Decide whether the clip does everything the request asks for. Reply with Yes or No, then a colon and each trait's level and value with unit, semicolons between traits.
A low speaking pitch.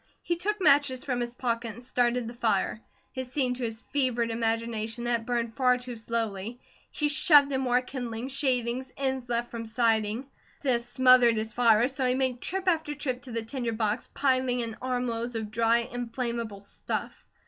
No: high, 245 Hz